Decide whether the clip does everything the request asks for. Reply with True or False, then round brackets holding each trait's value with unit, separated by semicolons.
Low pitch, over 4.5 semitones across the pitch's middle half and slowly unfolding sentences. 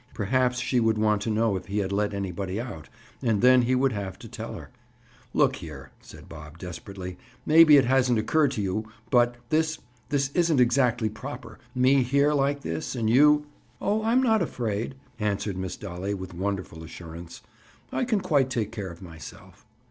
False (115 Hz; 5.4 semitones; 175 wpm)